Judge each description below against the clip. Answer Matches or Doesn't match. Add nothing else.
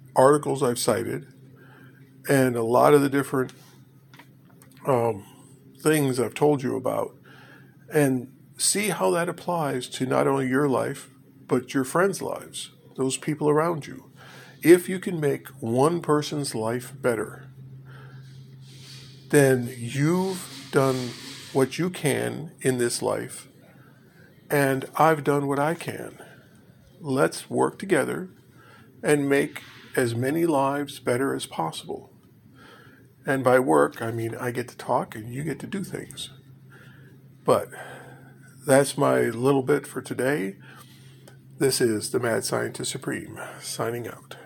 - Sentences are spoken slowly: Matches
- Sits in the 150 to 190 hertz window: Doesn't match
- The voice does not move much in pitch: Matches